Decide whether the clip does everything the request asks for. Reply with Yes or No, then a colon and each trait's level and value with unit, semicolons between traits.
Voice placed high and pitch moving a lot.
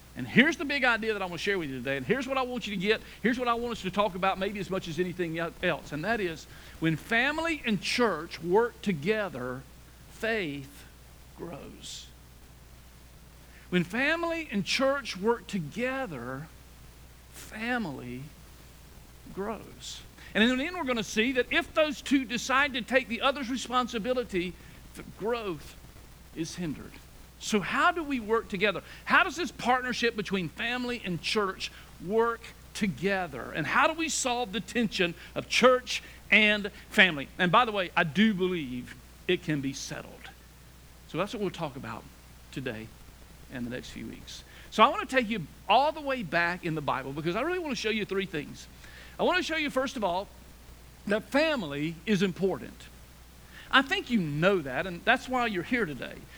Yes: high, 200 Hz; wide, 8.1 semitones